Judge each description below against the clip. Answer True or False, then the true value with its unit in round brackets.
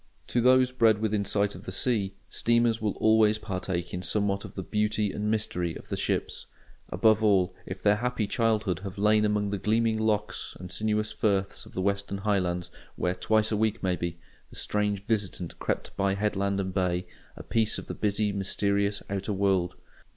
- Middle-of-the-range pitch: False (105 Hz)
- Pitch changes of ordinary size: False (2.0 semitones)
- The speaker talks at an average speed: True (185 wpm)